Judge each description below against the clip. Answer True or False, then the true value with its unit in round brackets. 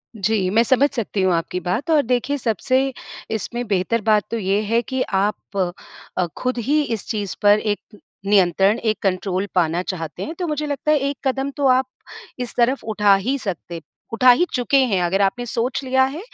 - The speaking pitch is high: True (225 Hz)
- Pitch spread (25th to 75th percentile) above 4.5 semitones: True (5.1 semitones)